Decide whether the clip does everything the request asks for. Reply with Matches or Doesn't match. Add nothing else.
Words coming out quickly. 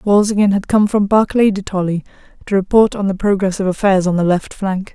Matches